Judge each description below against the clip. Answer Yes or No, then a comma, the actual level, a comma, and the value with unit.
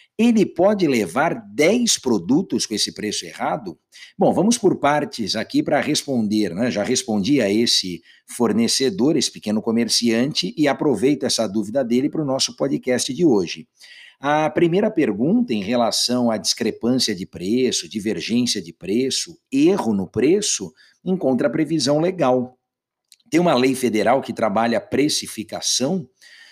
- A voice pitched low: Yes, low, 125 Hz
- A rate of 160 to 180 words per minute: No, average, 145 wpm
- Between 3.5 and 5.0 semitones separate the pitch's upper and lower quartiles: No, wide, 5.5 semitones